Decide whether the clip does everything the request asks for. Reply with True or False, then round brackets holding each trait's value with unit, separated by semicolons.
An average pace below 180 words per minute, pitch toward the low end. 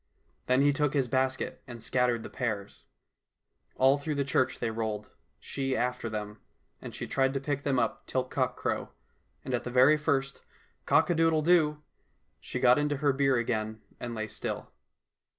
False (185 wpm; 130 Hz)